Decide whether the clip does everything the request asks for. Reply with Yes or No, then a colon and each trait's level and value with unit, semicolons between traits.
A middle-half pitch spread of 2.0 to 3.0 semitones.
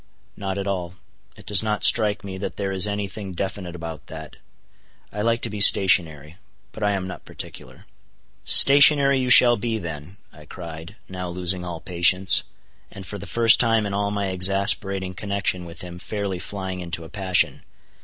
Yes: narrow, 2.6 semitones